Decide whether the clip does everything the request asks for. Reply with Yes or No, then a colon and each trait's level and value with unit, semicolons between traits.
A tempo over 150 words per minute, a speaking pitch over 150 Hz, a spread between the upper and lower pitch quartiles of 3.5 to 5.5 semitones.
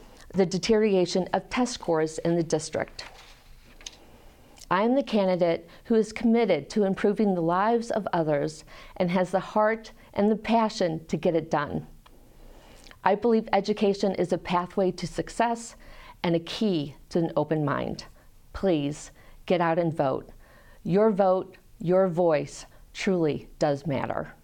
No: average, 145 wpm; medium, 185 Hz; average, 4.2 semitones